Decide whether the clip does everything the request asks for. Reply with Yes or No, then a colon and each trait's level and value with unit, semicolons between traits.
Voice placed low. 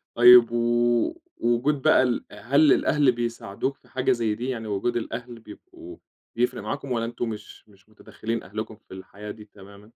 Yes: low, 120 Hz